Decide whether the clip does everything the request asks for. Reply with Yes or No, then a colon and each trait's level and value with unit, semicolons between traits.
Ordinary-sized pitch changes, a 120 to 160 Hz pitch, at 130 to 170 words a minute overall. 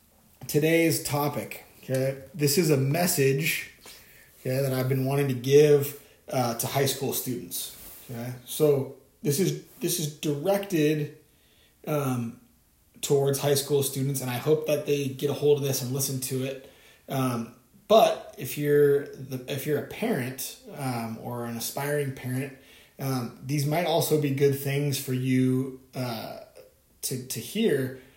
No: narrow, 2.2 semitones; medium, 140 Hz; average, 155 wpm